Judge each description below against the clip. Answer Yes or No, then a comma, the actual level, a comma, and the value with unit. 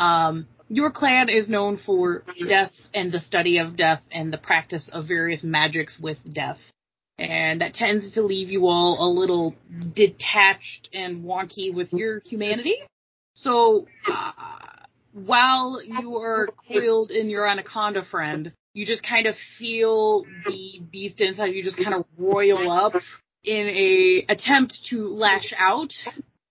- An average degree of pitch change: Yes, average, 4.2 semitones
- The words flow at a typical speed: Yes, average, 145 wpm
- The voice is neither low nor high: No, high, 200 Hz